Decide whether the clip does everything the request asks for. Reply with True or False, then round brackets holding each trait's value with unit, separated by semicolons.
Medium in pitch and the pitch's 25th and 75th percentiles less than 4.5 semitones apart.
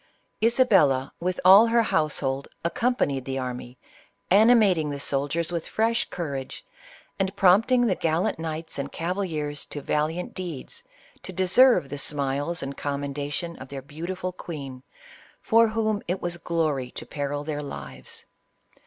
False (160 Hz; 5.0 semitones)